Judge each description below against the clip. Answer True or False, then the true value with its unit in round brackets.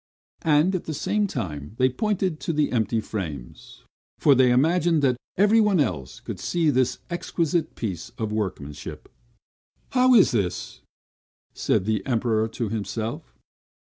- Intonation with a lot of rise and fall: True (7.9 semitones)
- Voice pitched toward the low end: True (130 Hz)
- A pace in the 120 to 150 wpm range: True (140 wpm)